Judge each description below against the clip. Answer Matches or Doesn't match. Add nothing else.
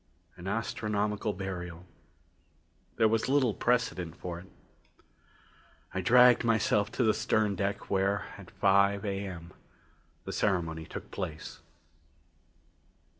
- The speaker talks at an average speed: Doesn't match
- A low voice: Matches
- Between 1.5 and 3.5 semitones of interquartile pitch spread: Matches